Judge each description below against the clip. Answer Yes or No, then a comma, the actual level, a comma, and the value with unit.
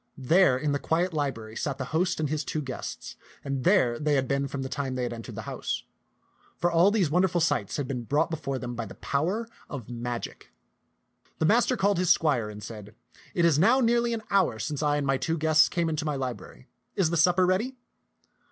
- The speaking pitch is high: No, medium, 150 Hz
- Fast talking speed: Yes, fast, 225 wpm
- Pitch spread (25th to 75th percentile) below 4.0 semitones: No, wide, 5.4 semitones